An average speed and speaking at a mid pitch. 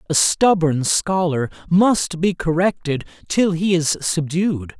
No: slow, 125 wpm; medium, 170 Hz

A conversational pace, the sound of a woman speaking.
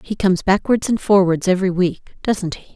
Yes: average, 175 wpm; female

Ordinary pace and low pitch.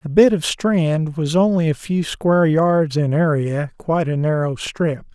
No: average, 185 wpm; medium, 160 Hz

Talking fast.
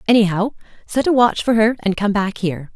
Yes: fast, 220 wpm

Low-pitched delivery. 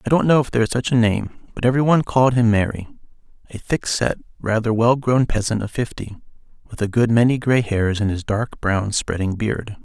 Yes: low, 115 Hz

